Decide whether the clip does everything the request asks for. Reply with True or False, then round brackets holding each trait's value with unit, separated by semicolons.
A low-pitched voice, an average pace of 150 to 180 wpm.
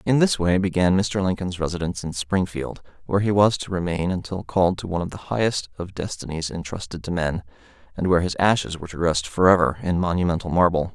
False (90 Hz; 205 wpm)